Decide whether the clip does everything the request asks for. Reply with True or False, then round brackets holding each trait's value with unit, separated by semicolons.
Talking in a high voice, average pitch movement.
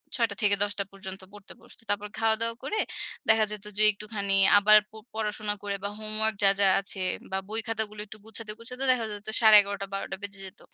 False (210 Hz; 1.6 semitones)